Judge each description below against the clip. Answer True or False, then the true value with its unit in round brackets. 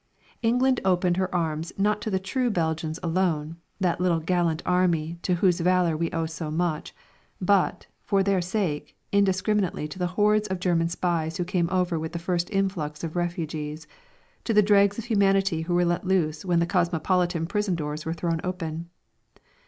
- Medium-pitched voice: True (175 Hz)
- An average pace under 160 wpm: False (175 wpm)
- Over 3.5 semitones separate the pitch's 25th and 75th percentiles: False (2.6 semitones)